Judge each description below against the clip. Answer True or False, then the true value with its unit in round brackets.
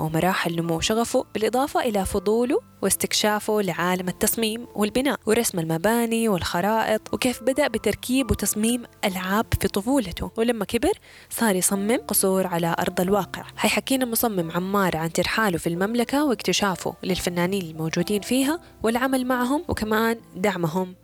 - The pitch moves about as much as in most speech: True (4.3 semitones)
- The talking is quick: False (125 wpm)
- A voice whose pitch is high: True (210 Hz)